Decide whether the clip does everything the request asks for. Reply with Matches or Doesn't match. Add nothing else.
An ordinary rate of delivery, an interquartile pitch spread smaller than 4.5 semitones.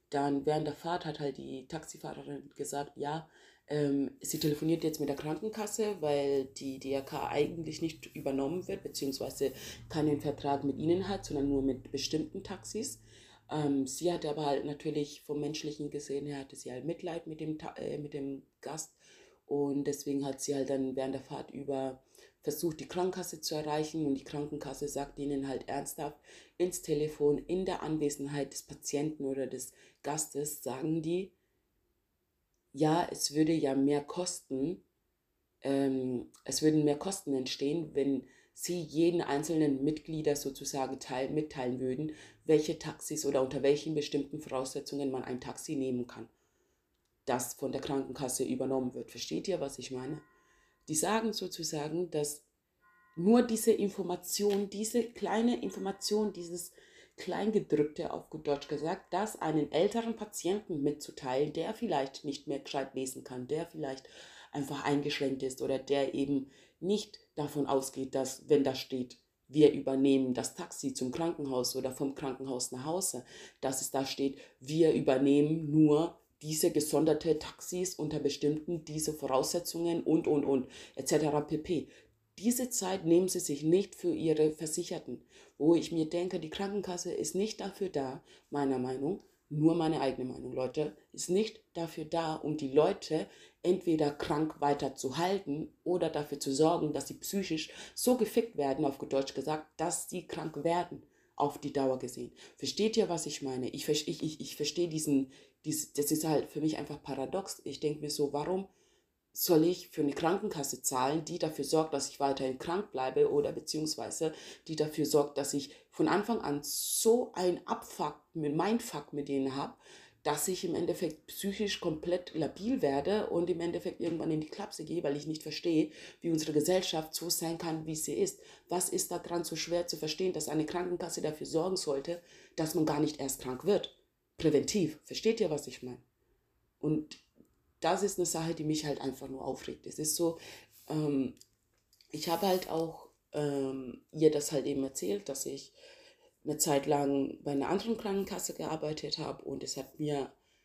Matches